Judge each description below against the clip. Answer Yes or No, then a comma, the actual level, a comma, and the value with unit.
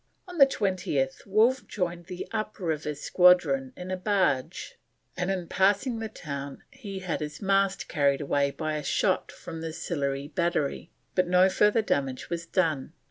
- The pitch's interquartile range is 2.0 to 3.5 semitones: No, average, 4.9 semitones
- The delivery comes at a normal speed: Yes, average, 160 wpm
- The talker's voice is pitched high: No, medium, 175 Hz